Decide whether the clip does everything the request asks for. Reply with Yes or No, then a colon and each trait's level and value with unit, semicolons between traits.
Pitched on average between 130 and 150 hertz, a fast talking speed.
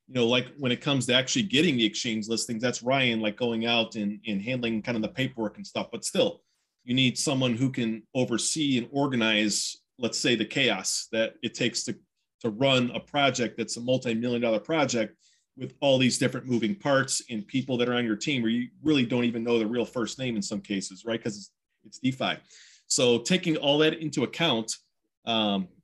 No: low, 120 Hz; fast, 210 wpm